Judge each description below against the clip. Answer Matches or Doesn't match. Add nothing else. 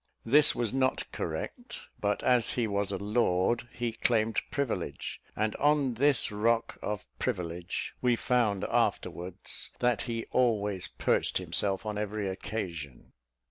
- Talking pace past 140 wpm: Doesn't match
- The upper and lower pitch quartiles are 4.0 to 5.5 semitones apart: Doesn't match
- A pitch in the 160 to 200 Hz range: Doesn't match